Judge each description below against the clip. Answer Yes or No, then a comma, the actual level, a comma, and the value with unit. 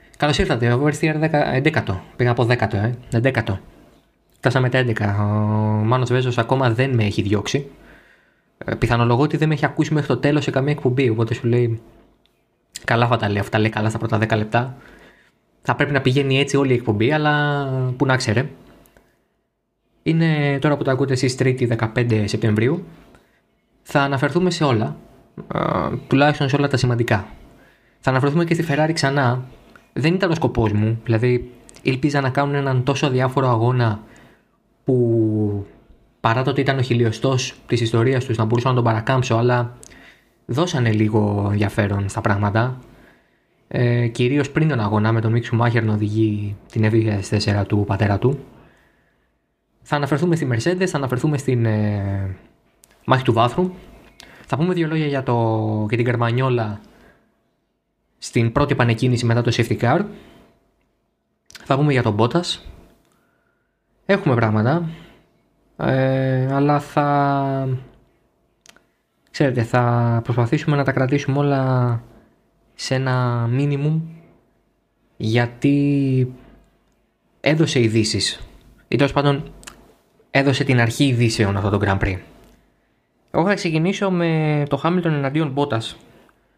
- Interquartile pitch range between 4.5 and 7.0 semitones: No, average, 3.9 semitones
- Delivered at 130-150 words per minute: Yes, average, 140 wpm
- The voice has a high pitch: No, low, 125 Hz